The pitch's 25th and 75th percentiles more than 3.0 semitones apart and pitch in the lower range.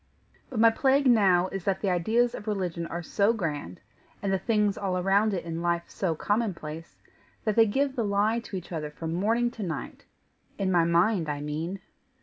No: average, 4.5 semitones; high, 195 Hz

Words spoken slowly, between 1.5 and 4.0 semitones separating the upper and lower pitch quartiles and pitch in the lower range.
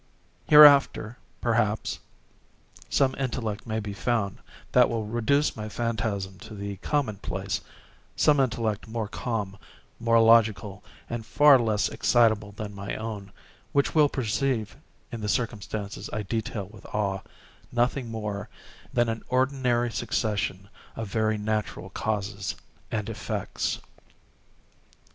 Yes: slow, 120 wpm; narrow, 2.5 semitones; low, 110 Hz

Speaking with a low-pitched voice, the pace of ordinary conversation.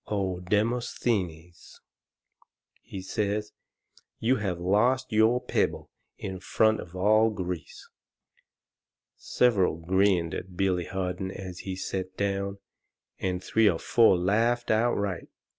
No: very low, 95 Hz; slow, 110 wpm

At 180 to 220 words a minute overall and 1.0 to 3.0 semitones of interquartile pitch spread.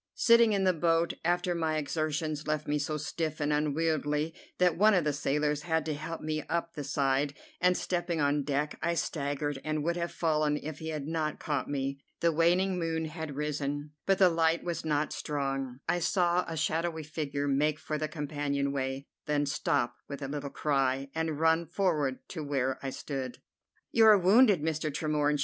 Yes: average, 190 wpm; narrow, 2.4 semitones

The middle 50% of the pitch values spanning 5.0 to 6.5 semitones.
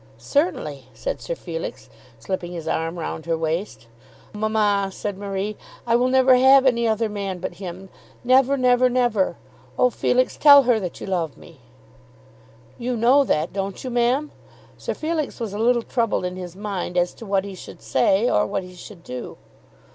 Yes: wide, 5.5 semitones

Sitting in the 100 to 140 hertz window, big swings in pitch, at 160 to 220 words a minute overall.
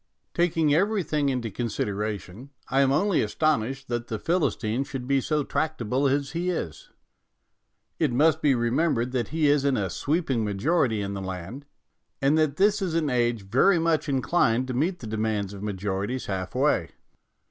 Yes: low, 135 Hz; wide, 6.0 semitones; average, 170 wpm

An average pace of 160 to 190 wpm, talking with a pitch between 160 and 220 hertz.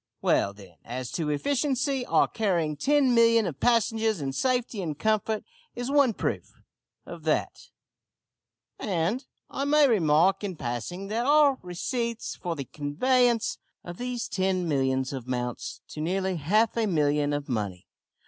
No: average, 145 wpm; high, 190 Hz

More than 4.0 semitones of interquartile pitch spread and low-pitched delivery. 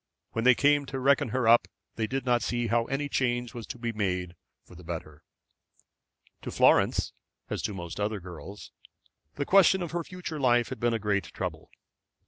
Yes: average, 4.7 semitones; low, 120 Hz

